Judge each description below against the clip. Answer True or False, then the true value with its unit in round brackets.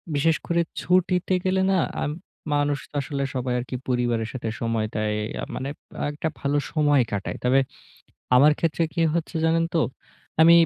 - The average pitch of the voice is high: False (145 Hz)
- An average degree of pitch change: True (5.0 semitones)